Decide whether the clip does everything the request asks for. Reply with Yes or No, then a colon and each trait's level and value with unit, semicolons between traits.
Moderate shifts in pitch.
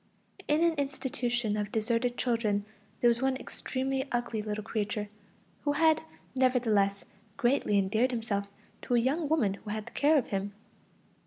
Yes: average, 4.1 semitones